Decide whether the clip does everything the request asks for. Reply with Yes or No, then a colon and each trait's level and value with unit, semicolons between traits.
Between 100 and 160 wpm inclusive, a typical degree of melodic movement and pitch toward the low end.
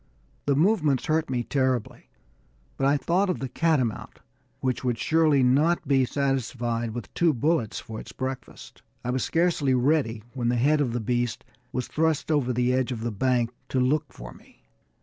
No: average, 180 wpm; average, 3.8 semitones; low, 130 Hz